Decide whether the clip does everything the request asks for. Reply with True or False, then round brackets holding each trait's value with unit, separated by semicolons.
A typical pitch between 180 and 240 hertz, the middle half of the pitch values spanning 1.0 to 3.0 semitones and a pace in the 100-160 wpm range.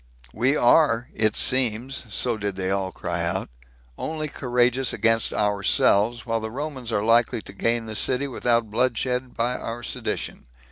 False (120 Hz; 2.5 semitones; 150 wpm)